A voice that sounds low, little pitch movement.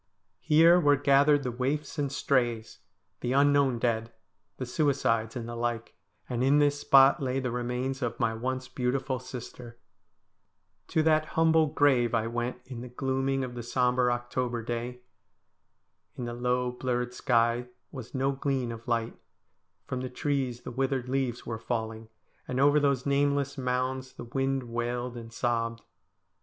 Yes: low, 125 Hz; narrow, 2.3 semitones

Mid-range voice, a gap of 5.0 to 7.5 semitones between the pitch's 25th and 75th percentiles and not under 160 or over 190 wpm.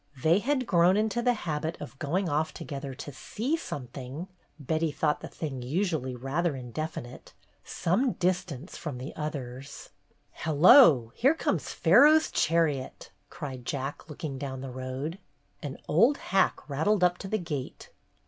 No: medium, 155 Hz; wide, 5.4 semitones; average, 150 wpm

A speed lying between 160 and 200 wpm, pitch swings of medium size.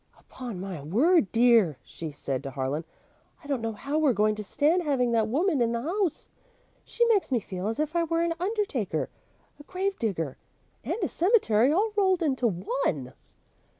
No: average, 185 wpm; wide, 9.0 semitones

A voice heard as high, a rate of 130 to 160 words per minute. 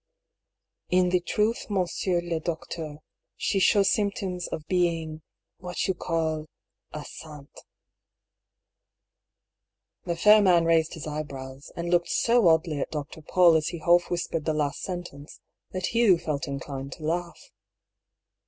No: medium, 170 Hz; average, 145 wpm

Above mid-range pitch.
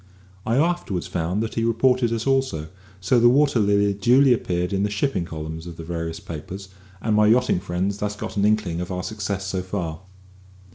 No: low, 100 Hz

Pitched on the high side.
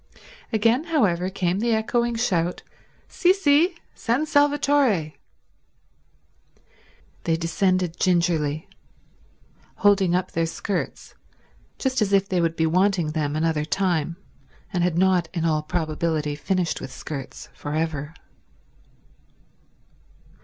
No: medium, 180 Hz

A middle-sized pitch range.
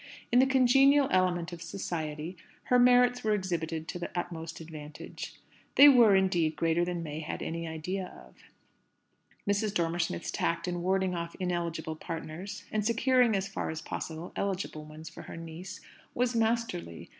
Yes: average, 4.7 semitones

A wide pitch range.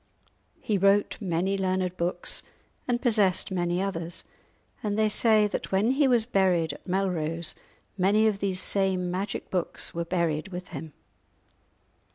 No: average, 2.8 semitones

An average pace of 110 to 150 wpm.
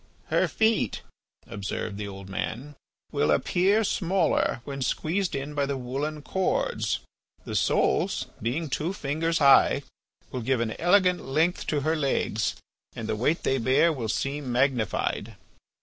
Yes: average, 145 wpm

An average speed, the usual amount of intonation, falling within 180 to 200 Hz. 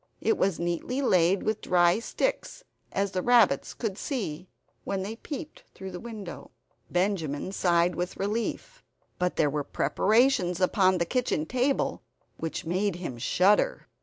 Yes: average, 145 wpm; average, 4.7 semitones; high, 190 Hz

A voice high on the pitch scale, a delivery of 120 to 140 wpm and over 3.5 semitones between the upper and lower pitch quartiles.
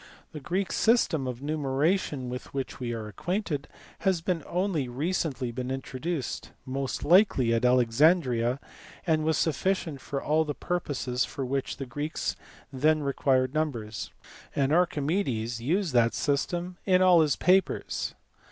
No: medium, 145 Hz; slow, 135 wpm; average, 5.1 semitones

